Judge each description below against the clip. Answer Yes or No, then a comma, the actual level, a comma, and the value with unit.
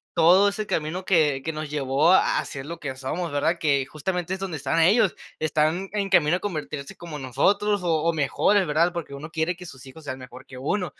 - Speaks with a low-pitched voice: No, medium, 160 Hz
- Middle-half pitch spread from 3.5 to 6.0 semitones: Yes, average, 3.9 semitones